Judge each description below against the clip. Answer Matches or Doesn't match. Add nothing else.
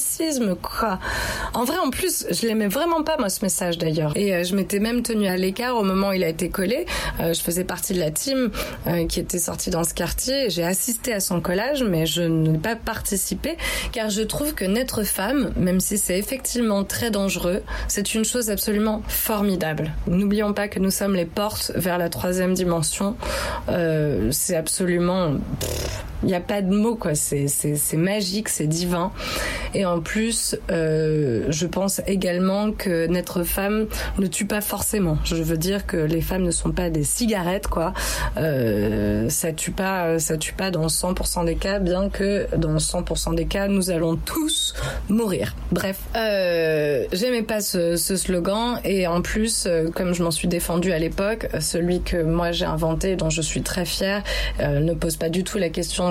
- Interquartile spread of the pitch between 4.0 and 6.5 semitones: Doesn't match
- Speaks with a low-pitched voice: Doesn't match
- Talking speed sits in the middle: Matches